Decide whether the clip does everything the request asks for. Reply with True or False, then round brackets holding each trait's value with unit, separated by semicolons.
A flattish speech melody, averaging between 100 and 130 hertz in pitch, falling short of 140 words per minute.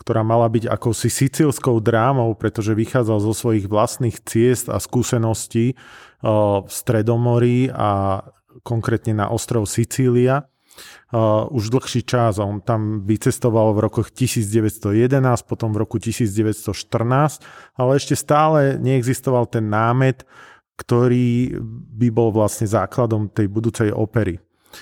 True (2.3 semitones; 115 Hz; 115 wpm)